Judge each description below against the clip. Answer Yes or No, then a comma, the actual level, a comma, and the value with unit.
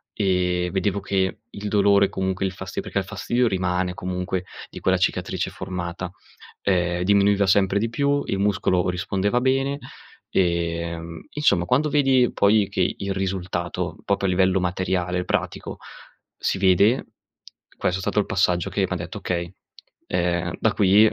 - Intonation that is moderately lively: No, narrow, 2.2 semitones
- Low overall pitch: Yes, very low, 95 Hz